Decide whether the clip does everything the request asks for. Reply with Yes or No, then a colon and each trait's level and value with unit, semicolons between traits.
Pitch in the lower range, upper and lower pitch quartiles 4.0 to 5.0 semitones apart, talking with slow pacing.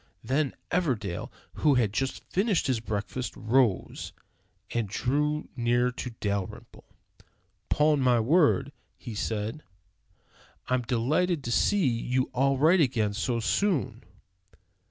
Yes: low, 125 Hz; average, 4.4 semitones; slow, 115 wpm